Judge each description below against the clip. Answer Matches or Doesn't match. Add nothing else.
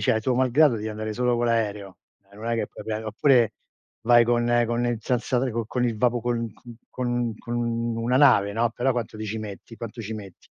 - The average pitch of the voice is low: Matches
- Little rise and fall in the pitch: Matches